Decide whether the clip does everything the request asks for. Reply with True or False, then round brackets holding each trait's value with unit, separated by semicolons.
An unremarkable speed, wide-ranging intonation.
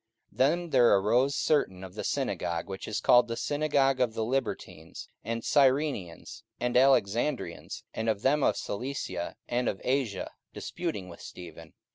True (155 wpm; 5.7 semitones)